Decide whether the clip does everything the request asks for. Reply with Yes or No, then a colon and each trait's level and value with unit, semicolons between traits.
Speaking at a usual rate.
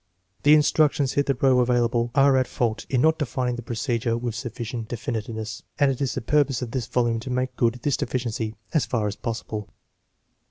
Yes: average, 185 wpm